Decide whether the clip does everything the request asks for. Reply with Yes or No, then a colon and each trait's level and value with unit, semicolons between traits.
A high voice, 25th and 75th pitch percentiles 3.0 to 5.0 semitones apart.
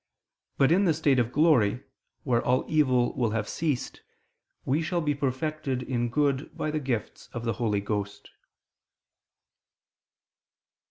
No: low, 130 Hz; average, 4.3 semitones